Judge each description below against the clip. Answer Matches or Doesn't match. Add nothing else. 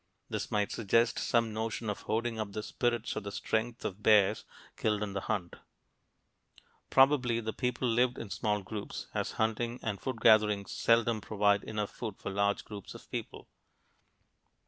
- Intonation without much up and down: Matches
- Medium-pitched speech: Doesn't match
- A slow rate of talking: Doesn't match